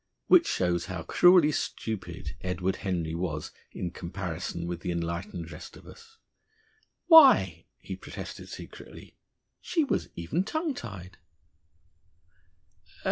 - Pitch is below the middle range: Yes, very low, 90 Hz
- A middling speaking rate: No, slow, 115 wpm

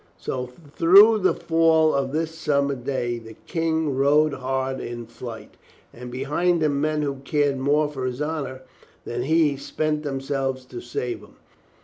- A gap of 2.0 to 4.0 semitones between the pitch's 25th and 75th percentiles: Yes, average, 3.0 semitones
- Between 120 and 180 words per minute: Yes, average, 155 wpm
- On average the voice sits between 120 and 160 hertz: Yes, medium, 140 Hz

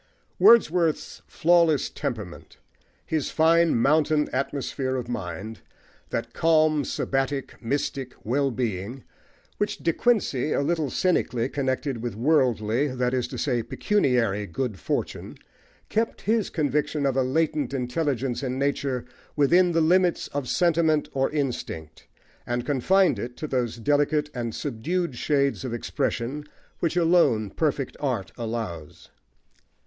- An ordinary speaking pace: No, slow, 125 wpm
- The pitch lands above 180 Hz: No, medium, 140 Hz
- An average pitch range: Yes, average, 4.4 semitones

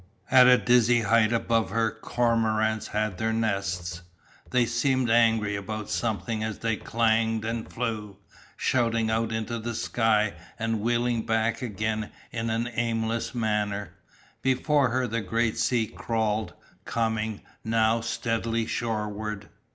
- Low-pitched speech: Yes, low, 115 Hz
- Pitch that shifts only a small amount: Yes, narrow, 1.3 semitones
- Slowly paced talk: Yes, slow, 130 wpm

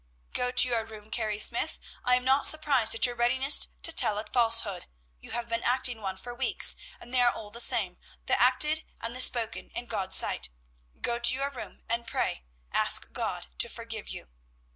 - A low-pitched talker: No, high, 240 Hz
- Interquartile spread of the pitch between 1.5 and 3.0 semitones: Yes, narrow, 2.4 semitones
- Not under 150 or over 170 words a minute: No, fast, 205 wpm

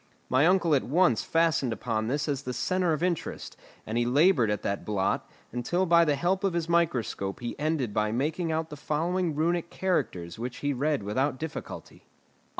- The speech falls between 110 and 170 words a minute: No, average, 185 wpm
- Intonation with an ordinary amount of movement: No, wide, 5.7 semitones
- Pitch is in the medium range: Yes, medium, 150 Hz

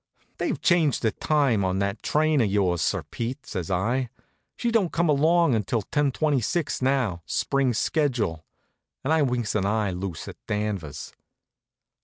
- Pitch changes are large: Yes, wide, 6.9 semitones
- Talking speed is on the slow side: No, average, 160 wpm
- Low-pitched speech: Yes, low, 120 Hz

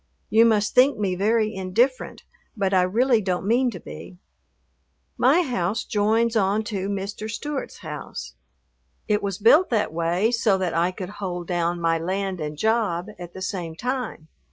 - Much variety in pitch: No, average, 4.0 semitones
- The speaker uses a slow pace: No, average, 165 wpm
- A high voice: Yes, high, 200 Hz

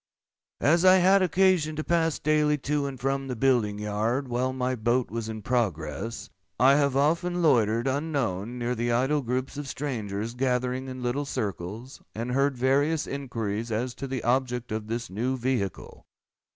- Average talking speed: Yes, average, 165 wpm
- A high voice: No, low, 130 Hz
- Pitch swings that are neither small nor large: Yes, average, 3.5 semitones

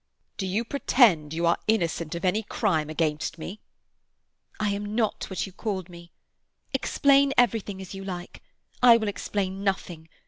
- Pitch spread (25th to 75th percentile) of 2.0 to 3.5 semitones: No, average, 4.1 semitones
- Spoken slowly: No, average, 160 wpm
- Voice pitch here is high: Yes, high, 195 Hz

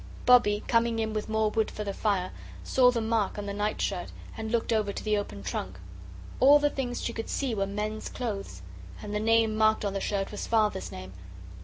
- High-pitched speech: Yes, high, 215 Hz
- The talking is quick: Yes, fast, 215 wpm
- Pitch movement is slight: Yes, narrow, 2.1 semitones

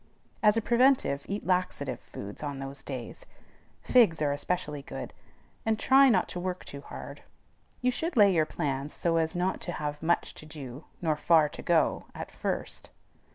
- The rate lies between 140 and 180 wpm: Yes, average, 175 wpm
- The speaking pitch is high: No, medium, 165 Hz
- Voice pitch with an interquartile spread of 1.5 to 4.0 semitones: No, wide, 5.6 semitones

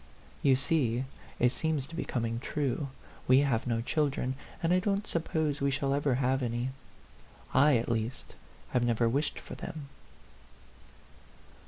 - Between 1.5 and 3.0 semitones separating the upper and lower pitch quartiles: No, average, 3.6 semitones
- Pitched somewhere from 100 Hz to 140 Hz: Yes, low, 135 Hz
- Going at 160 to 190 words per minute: No, average, 150 wpm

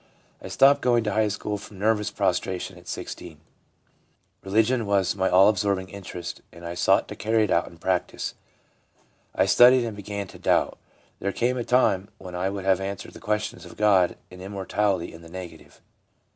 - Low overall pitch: Yes, low, 100 Hz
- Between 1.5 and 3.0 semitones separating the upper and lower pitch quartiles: Yes, narrow, 2.5 semitones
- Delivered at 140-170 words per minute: No, average, 185 wpm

